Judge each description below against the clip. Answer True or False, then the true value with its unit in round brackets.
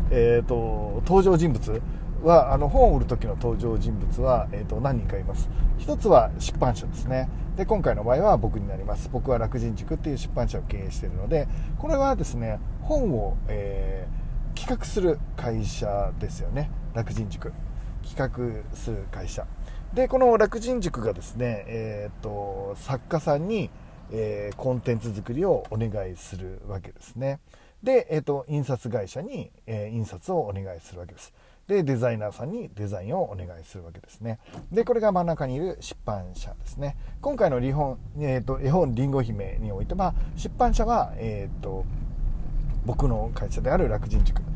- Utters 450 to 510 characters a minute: False (325 characters per minute)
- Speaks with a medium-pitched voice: False (120 Hz)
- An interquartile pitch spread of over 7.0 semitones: False (5.9 semitones)